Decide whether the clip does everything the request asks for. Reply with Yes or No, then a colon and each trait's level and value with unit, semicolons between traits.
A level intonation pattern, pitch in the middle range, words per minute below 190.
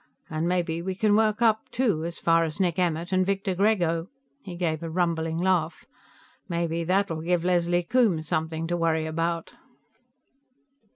Yes: narrow, 2.3 semitones; medium, 170 Hz; average, 160 wpm